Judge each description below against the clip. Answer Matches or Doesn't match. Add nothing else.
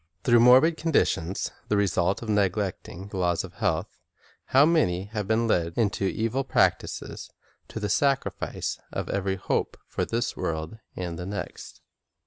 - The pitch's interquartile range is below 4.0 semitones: Doesn't match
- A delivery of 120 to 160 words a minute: Matches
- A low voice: Matches